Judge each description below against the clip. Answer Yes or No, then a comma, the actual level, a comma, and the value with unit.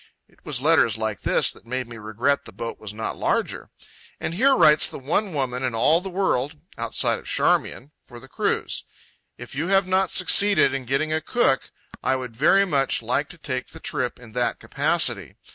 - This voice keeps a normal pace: Yes, average, 190 wpm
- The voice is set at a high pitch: No, low, 135 Hz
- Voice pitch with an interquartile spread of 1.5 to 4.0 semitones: No, average, 5.2 semitones